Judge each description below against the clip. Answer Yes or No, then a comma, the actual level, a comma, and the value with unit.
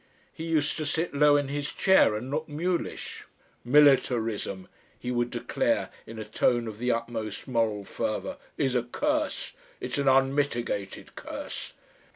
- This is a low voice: Yes, low, 130 Hz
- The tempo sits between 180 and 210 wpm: No, average, 150 wpm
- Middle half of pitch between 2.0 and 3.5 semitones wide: No, average, 4.3 semitones